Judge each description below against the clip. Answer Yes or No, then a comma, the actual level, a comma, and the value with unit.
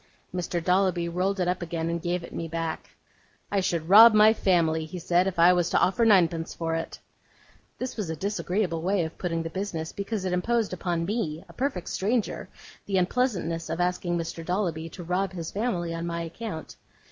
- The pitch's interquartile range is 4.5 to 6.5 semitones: No, average, 2.9 semitones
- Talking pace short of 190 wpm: No, average, 195 wpm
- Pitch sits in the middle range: Yes, medium, 180 Hz